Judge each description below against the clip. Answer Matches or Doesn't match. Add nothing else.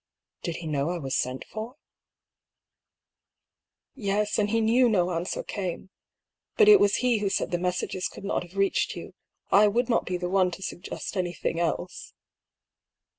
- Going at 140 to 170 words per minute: Doesn't match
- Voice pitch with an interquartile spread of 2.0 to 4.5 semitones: Matches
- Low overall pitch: Doesn't match